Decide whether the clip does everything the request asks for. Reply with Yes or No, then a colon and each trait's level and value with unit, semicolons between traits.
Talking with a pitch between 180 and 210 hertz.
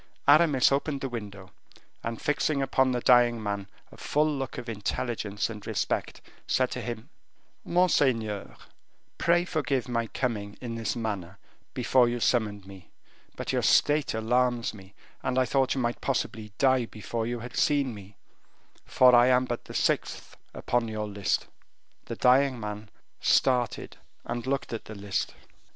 No: low, 120 Hz